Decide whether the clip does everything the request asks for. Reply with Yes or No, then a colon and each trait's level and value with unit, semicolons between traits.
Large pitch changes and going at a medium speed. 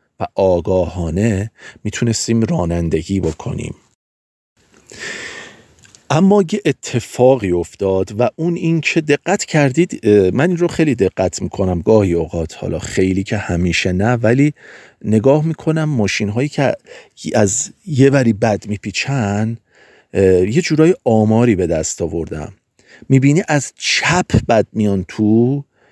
Yes: wide, 7.2 semitones; average, 115 wpm